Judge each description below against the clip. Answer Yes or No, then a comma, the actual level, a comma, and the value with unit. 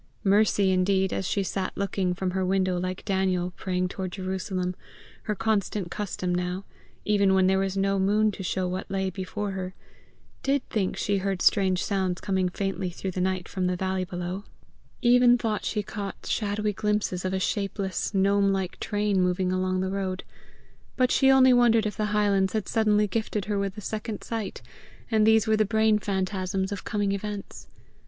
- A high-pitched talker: Yes, high, 195 Hz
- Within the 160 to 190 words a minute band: Yes, average, 180 wpm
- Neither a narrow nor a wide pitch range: No, narrow, 2.0 semitones